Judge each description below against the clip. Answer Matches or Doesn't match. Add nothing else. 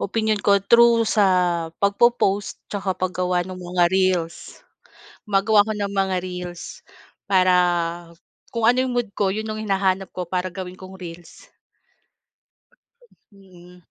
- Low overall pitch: Doesn't match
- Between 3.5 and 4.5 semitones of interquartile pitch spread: Doesn't match